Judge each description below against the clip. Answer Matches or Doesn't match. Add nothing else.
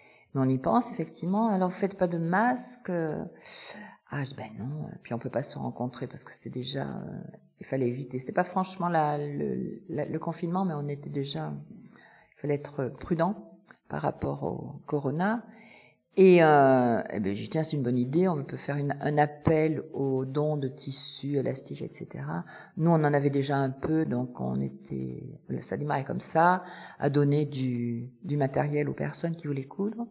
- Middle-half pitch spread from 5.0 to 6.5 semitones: Doesn't match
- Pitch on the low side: Doesn't match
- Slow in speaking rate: Doesn't match